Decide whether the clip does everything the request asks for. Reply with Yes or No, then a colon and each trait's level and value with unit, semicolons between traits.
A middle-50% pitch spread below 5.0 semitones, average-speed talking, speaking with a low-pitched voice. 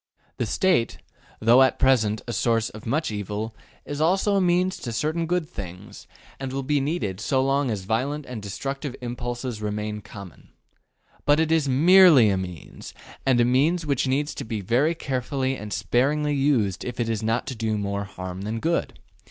No: wide, 5.4 semitones; average, 185 wpm; low, 125 Hz